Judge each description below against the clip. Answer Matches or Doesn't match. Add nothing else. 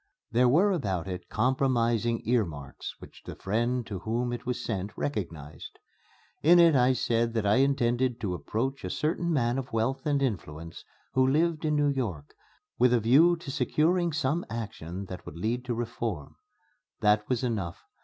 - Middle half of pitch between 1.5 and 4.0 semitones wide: Doesn't match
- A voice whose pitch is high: Doesn't match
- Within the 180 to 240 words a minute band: Doesn't match